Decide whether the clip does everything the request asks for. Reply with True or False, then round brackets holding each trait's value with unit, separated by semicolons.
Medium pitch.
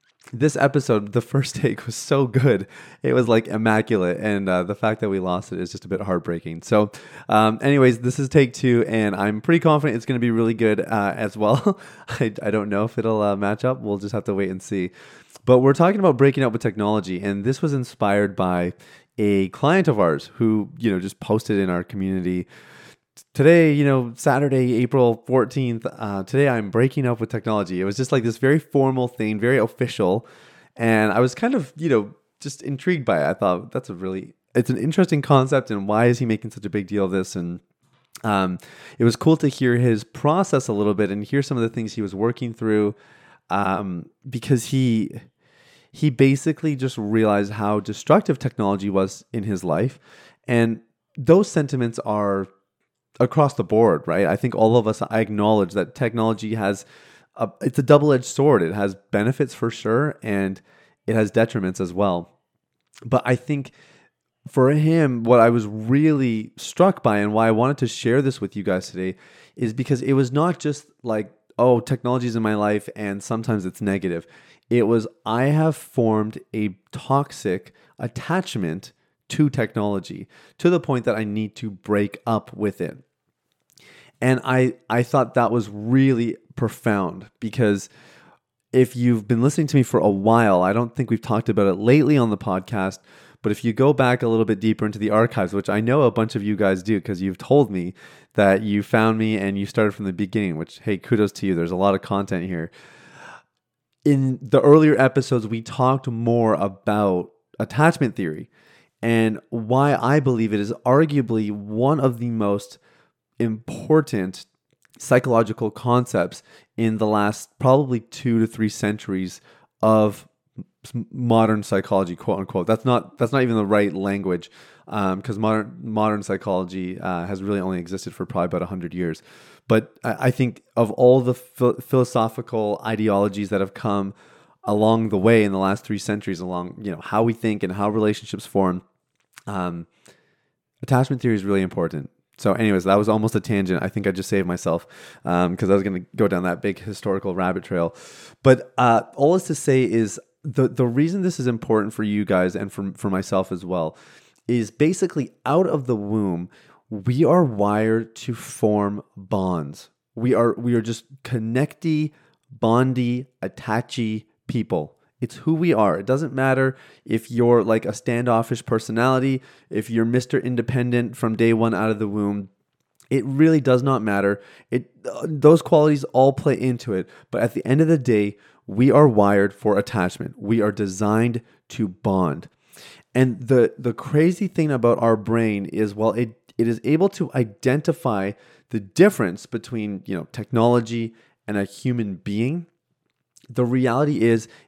False (115 Hz)